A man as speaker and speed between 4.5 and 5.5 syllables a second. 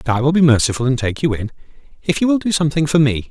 No: male; 7.4 syllables/s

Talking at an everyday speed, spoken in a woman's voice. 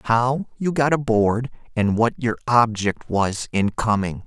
No: average, 155 wpm; male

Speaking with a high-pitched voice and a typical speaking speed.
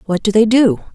No: high, 210 Hz; fast, 255 wpm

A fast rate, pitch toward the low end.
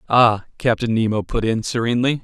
No: average, 160 wpm; low, 115 Hz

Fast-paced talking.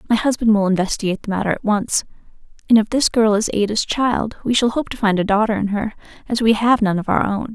Yes: fast, 245 wpm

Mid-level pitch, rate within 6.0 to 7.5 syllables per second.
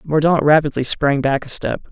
No: medium, 145 Hz; 5.1 syllables/s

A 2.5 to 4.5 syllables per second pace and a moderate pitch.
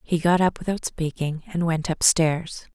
Yes: 4.4 syllables/s; medium, 165 Hz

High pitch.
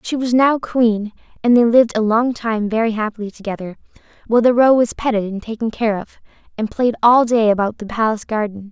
Yes: high, 225 Hz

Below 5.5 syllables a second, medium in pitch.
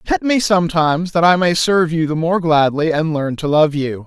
Yes: 5.3 syllables/s; medium, 165 Hz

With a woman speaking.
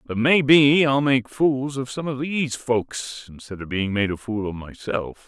No: male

